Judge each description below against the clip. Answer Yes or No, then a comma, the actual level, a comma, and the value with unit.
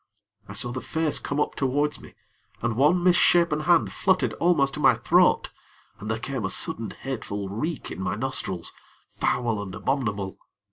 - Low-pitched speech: Yes, low, 130 Hz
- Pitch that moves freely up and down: Yes, wide, 6.4 semitones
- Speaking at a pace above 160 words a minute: Yes, average, 170 wpm